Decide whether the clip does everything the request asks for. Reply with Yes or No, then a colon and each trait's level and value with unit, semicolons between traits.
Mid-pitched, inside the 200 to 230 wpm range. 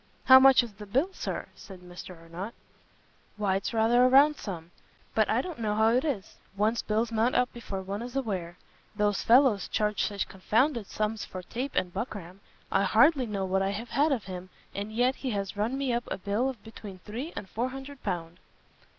No: high, 220 Hz; fast, 205 wpm